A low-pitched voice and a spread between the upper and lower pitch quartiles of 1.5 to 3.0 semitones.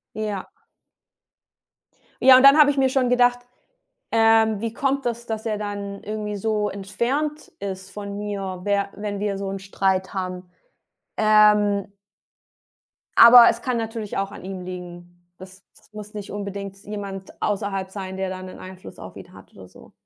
No: high, 205 Hz; narrow, 2.6 semitones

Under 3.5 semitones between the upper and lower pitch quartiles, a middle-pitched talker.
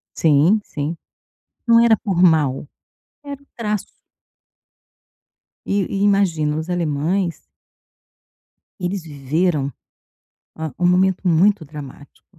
No: average, 4.6 semitones; medium, 170 Hz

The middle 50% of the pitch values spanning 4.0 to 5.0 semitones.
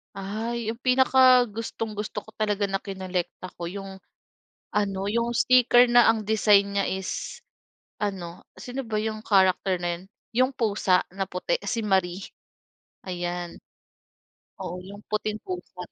No: average, 3.4 semitones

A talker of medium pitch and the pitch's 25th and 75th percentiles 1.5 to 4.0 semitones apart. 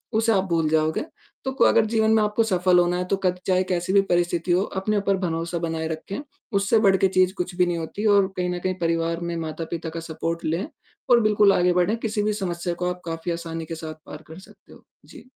Yes: medium, 180 Hz; average, 2.9 semitones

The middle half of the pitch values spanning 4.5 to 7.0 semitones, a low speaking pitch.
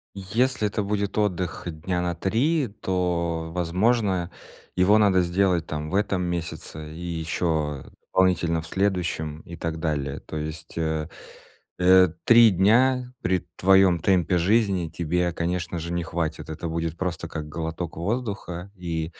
No: average, 2.9 semitones; very low, 90 Hz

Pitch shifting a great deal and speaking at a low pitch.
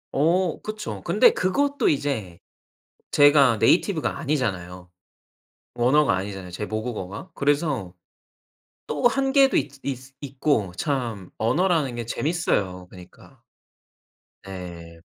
Yes: wide, 8.3 semitones; low, 130 Hz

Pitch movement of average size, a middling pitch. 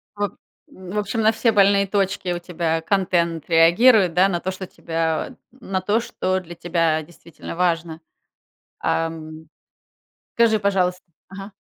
Yes: average, 3.2 semitones; medium, 180 Hz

